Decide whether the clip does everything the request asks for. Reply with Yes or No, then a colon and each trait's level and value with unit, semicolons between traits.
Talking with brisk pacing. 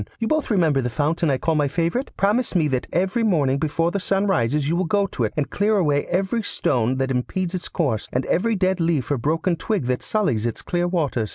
Yes: fast, 235 wpm